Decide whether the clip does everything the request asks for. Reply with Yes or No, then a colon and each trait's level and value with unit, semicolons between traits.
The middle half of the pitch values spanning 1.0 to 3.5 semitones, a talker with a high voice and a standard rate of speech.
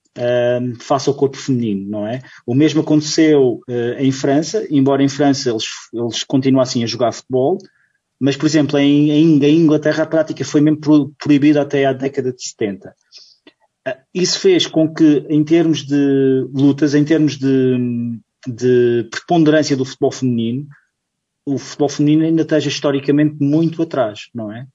No: average, 2.9 semitones; medium, 140 Hz; average, 150 wpm